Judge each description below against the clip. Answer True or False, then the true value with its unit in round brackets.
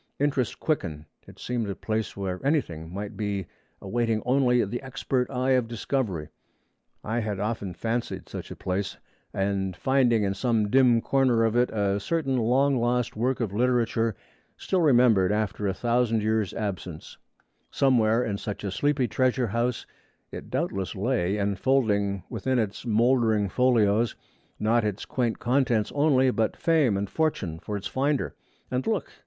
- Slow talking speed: False (155 wpm)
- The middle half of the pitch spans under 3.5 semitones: False (4.0 semitones)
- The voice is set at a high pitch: False (115 Hz)